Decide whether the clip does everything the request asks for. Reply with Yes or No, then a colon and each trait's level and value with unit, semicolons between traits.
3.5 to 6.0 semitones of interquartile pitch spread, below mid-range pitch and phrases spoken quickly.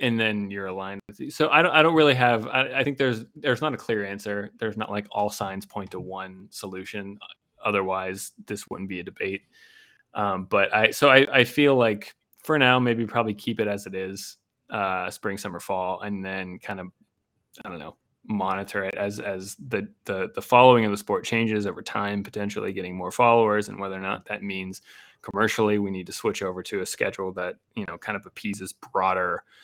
Yes: average, 3.8 semitones; low, 105 Hz; fast, 215 wpm